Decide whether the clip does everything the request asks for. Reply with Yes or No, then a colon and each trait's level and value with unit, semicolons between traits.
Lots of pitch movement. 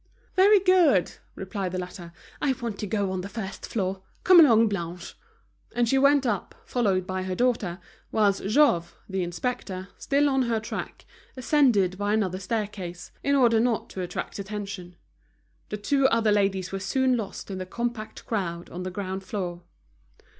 No: average, 4.4 semitones